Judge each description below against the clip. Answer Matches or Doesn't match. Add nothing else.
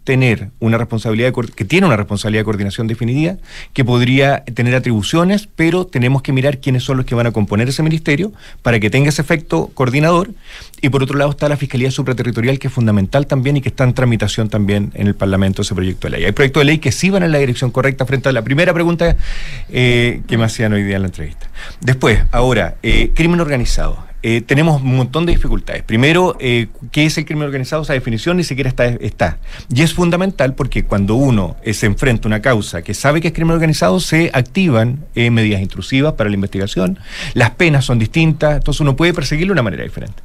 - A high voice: Doesn't match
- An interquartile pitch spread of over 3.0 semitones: Matches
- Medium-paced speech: Doesn't match